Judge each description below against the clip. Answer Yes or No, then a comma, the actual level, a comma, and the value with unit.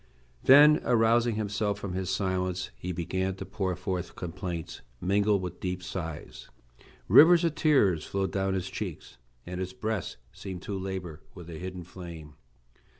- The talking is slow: No, average, 150 wpm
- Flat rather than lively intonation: Yes, narrow, 2.3 semitones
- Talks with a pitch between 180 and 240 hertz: No, very low, 95 Hz